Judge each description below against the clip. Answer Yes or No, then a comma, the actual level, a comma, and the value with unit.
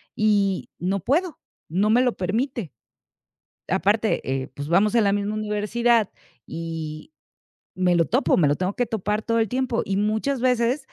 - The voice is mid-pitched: No, high, 210 Hz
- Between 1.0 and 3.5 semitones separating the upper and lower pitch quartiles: No, average, 4.2 semitones